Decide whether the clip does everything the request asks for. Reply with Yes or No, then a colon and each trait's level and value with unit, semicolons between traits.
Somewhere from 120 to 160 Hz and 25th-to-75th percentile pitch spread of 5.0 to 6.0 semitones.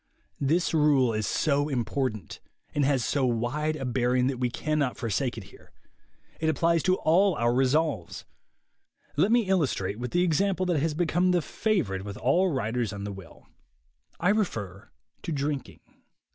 Yes: medium, 140 Hz; wide, 5.5 semitones